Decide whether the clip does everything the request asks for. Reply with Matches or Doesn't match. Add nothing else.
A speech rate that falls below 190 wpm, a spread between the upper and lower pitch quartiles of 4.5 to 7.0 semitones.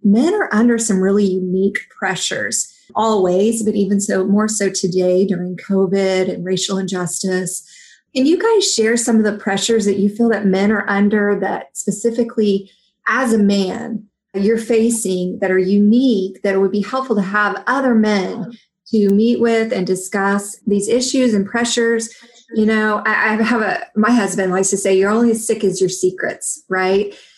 Doesn't match